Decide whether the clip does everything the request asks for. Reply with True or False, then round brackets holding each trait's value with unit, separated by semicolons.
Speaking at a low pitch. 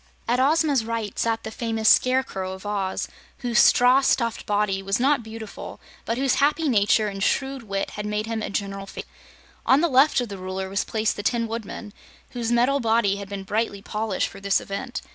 False (220 Hz)